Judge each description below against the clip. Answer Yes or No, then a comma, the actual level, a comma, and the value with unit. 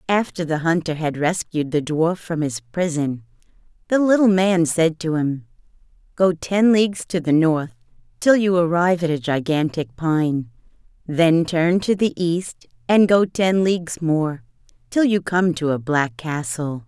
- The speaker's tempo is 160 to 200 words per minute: Yes, average, 165 wpm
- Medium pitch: Yes, medium, 165 Hz